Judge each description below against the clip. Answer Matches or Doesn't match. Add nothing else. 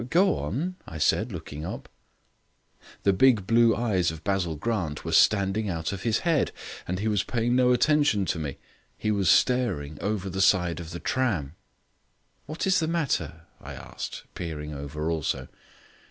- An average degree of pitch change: Doesn't match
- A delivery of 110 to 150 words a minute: Doesn't match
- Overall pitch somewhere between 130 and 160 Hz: Doesn't match